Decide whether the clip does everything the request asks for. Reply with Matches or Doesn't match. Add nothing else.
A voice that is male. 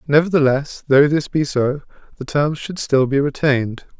Matches